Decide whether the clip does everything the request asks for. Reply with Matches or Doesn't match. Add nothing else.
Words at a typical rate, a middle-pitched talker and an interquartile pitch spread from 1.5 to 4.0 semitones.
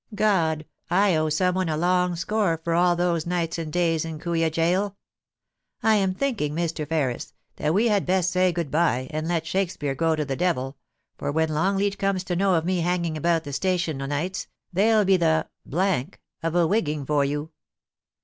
Matches